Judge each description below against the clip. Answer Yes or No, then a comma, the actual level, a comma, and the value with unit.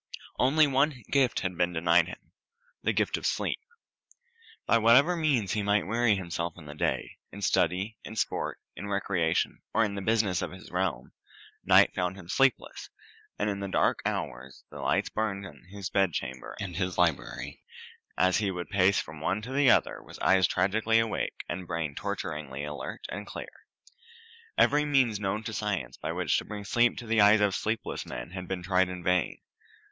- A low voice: Yes, low, 100 Hz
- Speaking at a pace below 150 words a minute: No, average, 185 wpm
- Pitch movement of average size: Yes, average, 3.8 semitones